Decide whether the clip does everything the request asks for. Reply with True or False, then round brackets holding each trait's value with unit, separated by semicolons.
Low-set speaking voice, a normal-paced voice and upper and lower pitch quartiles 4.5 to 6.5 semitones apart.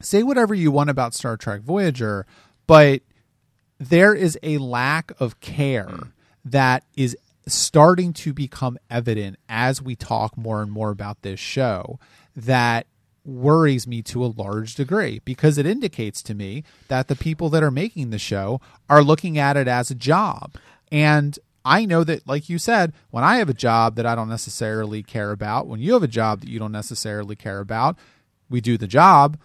True (130 Hz; 185 wpm; 5.3 semitones)